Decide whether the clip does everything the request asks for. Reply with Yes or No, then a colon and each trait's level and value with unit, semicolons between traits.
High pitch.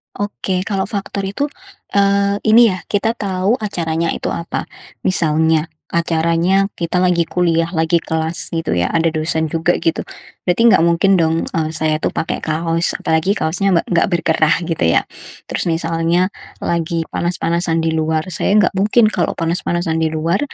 No: medium, 170 Hz